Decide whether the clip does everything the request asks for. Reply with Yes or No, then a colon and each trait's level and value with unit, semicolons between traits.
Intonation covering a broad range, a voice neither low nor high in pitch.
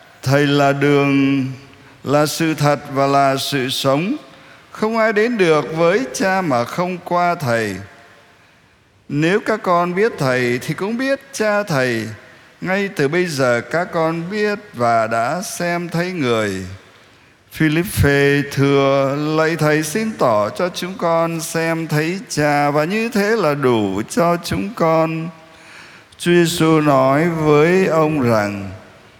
No: average, 4.3 semitones; medium, 155 Hz